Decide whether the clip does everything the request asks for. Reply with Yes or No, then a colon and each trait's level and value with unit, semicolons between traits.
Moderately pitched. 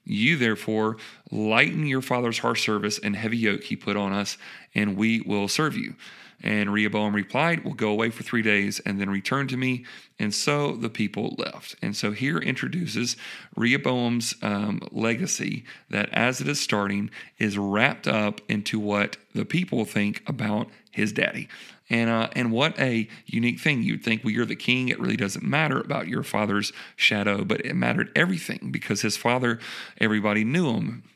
No: low, 110 Hz